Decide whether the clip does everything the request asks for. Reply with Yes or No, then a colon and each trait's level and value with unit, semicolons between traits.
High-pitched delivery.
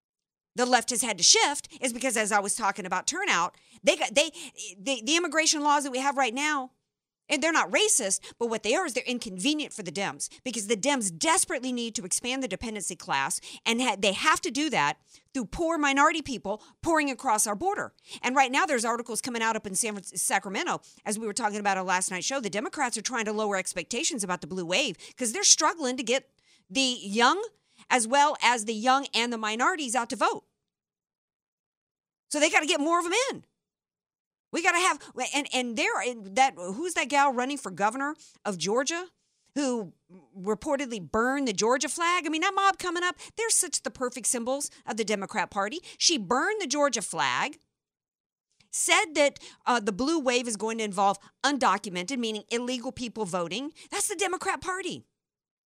Yes: very high, 255 Hz